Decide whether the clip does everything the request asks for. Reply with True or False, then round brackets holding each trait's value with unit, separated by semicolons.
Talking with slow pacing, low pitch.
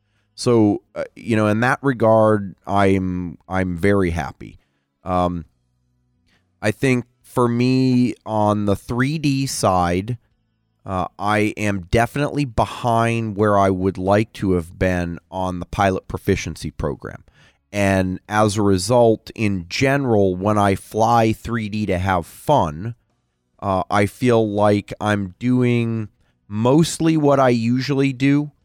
True (130 wpm; 105 Hz)